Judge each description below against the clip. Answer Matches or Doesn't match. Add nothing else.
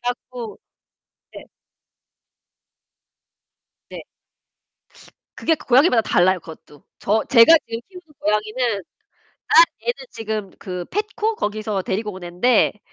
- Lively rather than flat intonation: Doesn't match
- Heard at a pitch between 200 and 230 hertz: Matches